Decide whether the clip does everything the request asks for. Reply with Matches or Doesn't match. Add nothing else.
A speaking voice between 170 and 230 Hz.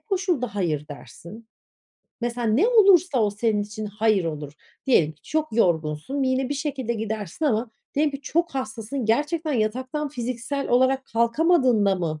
Doesn't match